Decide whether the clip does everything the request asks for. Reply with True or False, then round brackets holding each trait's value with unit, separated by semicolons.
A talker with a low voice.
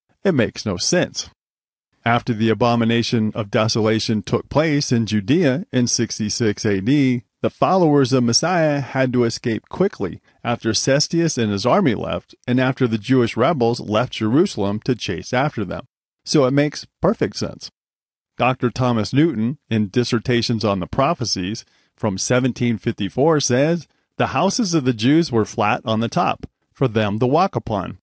True (120 Hz)